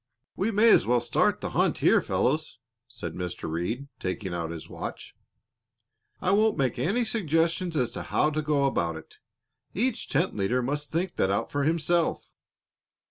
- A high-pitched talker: No, medium, 145 Hz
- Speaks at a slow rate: No, average, 170 wpm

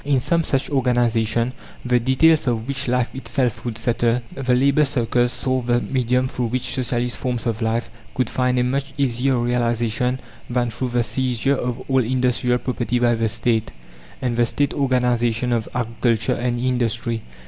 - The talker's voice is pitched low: Yes, low, 125 Hz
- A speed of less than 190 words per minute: Yes, average, 170 wpm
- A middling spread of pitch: No, narrow, 1.6 semitones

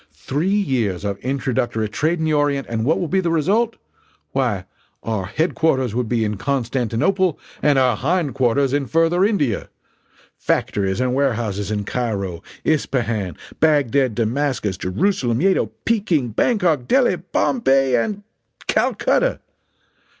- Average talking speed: No, slow, 130 wpm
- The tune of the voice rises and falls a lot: Yes, wide, 6.2 semitones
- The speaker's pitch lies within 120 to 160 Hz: Yes, low, 135 Hz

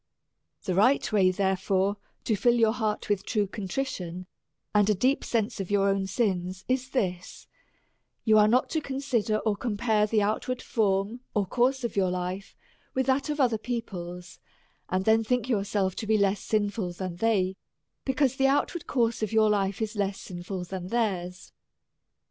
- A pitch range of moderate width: Yes, average, 3.7 semitones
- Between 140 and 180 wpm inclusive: Yes, average, 175 wpm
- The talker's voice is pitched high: Yes, high, 210 Hz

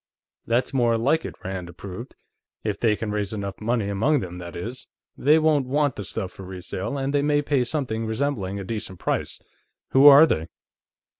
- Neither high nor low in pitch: No, low, 115 Hz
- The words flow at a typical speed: Yes, average, 190 wpm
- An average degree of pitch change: No, wide, 6.2 semitones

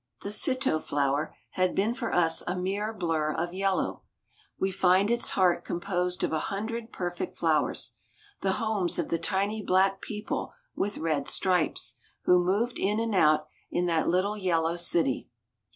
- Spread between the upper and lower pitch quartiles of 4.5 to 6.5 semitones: No, average, 3.4 semitones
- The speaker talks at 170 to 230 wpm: No, average, 160 wpm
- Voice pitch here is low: No, medium, 185 Hz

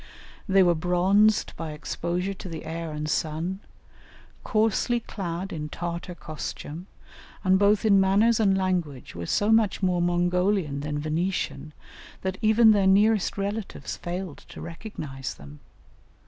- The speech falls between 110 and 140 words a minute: Yes, slow, 135 wpm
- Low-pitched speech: No, medium, 180 Hz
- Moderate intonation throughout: Yes, average, 3.8 semitones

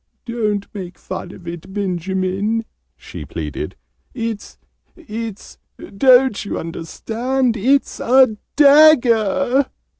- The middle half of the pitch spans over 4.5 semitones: Yes, average, 4.9 semitones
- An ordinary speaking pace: No, slow, 95 wpm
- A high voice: Yes, high, 225 Hz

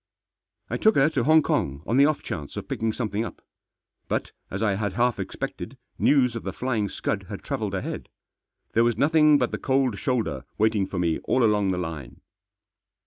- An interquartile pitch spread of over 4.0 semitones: Yes, average, 5.1 semitones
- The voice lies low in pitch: Yes, low, 115 Hz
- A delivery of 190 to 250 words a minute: Yes, average, 195 wpm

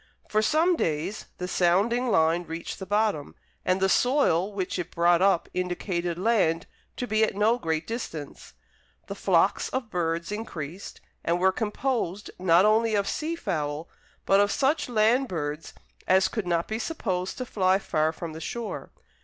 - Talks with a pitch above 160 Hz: Yes, high, 190 Hz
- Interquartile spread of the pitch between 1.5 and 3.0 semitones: No, average, 4.6 semitones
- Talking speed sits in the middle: Yes, average, 165 wpm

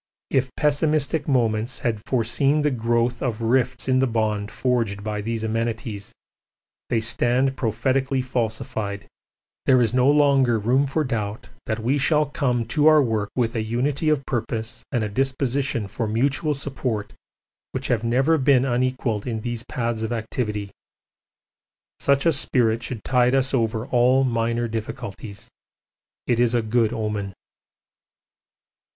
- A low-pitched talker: Yes, low, 120 Hz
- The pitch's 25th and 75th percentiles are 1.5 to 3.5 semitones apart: Yes, average, 3.1 semitones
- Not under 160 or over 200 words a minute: No, average, 145 wpm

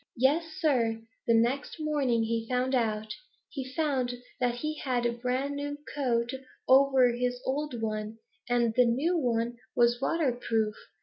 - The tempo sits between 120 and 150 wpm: Yes, average, 145 wpm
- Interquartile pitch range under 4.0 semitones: Yes, average, 3.0 semitones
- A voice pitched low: No, very high, 250 Hz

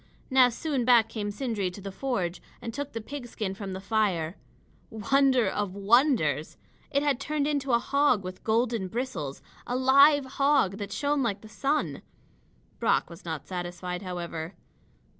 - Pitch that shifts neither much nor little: No, wide, 6.0 semitones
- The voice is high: Yes, high, 225 Hz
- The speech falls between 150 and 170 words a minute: Yes, average, 160 wpm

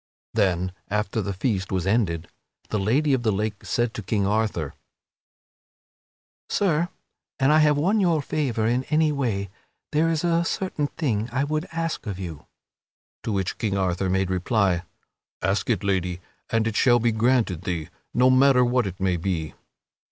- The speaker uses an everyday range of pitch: No, wide, 6.4 semitones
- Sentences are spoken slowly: No, average, 170 wpm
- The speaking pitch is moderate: No, low, 110 Hz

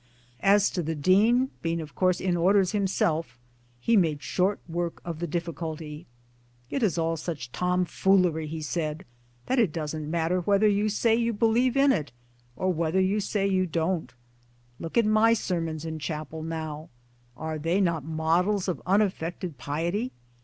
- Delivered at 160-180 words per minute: Yes, average, 165 wpm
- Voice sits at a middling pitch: Yes, medium, 175 Hz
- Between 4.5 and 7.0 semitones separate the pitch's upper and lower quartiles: No, average, 3.8 semitones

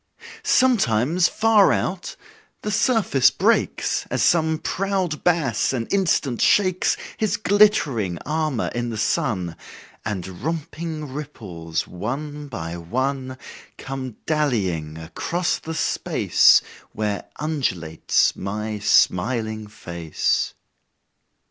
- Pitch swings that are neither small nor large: No, wide, 7.8 semitones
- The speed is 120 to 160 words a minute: No, slow, 100 wpm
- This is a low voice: Yes, low, 130 Hz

